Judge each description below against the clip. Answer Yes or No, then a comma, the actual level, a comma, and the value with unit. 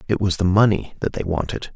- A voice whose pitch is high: No, very low, 95 Hz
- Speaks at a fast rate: Yes, fast, 240 wpm